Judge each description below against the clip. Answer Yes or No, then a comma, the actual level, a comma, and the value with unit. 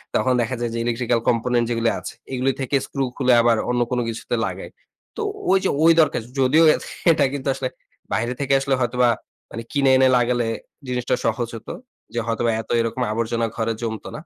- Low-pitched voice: Yes, low, 120 Hz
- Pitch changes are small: Yes, narrow, 2.2 semitones